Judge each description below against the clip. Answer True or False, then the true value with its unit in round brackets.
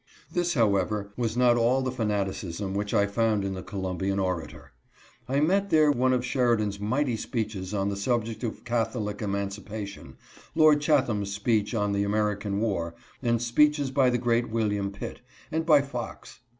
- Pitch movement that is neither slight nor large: True (3.9 semitones)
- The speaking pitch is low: True (110 Hz)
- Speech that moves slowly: False (160 wpm)